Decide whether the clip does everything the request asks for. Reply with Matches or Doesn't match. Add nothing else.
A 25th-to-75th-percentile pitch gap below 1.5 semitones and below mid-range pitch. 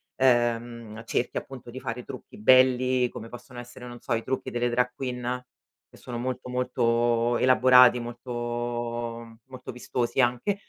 Matches